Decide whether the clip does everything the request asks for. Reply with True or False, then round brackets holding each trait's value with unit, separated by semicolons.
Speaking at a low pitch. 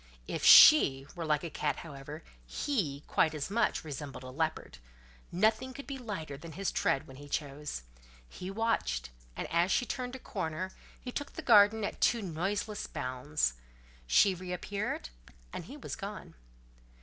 False (170 Hz)